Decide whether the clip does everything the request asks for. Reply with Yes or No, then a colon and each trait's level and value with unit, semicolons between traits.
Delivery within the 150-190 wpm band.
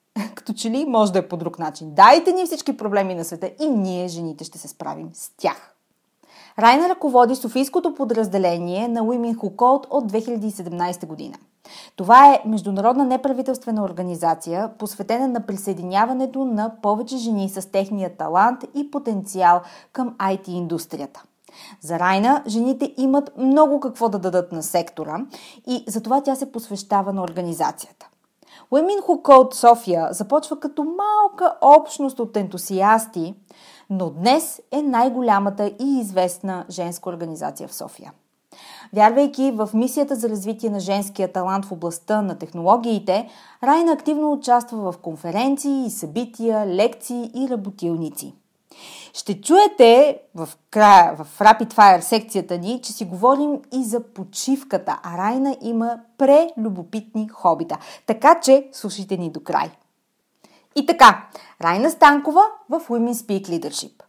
No: average, 135 wpm